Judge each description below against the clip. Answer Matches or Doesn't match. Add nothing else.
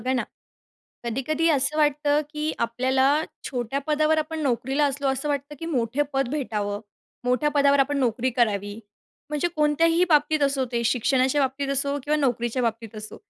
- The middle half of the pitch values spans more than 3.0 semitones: Matches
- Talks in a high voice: Matches